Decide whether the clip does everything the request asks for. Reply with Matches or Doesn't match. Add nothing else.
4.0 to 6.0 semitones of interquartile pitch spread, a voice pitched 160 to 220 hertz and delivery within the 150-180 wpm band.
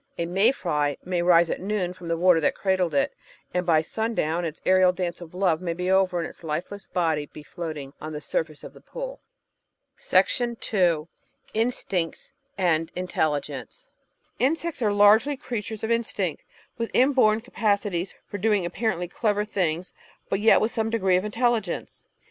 Matches